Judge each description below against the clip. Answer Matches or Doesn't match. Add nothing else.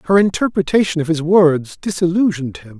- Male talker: Matches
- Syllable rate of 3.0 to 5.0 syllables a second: Doesn't match